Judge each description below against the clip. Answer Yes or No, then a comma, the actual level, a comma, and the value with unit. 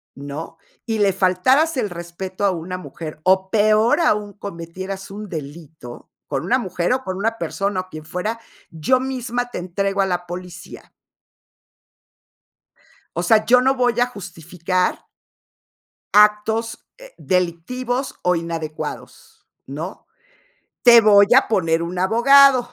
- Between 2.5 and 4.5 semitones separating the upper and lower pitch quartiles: No, average, 5.0 semitones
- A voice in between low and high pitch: No, high, 195 Hz